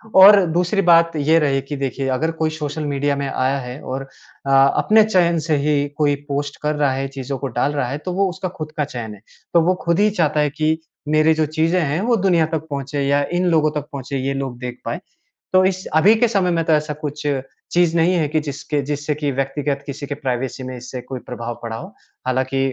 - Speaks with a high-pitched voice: No, medium, 150 Hz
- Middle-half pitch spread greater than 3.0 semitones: Yes, average, 3.5 semitones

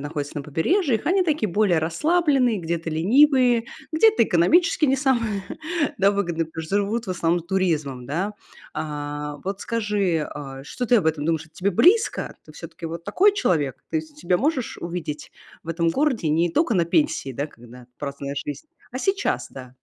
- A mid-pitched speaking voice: Yes, medium, 180 Hz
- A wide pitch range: Yes, wide, 8.6 semitones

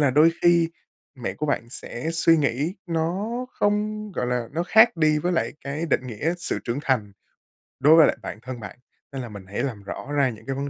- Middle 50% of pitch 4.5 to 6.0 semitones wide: Yes, average, 5.1 semitones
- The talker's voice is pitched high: No, medium, 145 Hz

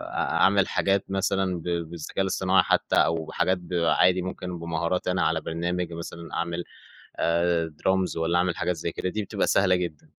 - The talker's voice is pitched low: Yes, very low, 90 Hz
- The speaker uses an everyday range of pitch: No, narrow, 1.7 semitones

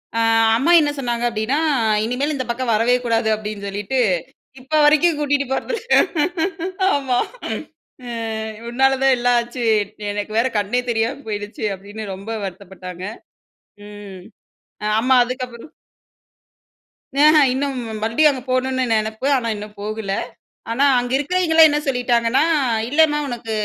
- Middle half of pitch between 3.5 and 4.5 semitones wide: Yes, average, 4.0 semitones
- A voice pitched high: Yes, high, 245 Hz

